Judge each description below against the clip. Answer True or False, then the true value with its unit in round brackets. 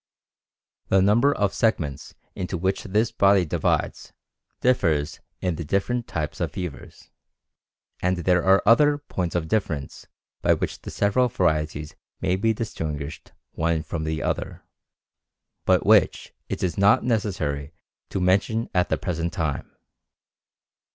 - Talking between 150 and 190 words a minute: False (135 wpm)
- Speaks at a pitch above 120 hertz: False (90 Hz)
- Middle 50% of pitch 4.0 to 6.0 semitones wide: True (4.6 semitones)